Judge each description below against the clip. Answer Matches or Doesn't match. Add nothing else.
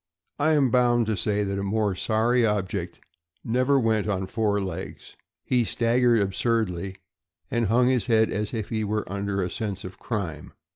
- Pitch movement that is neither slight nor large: Matches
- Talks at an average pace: Matches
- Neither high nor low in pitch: Doesn't match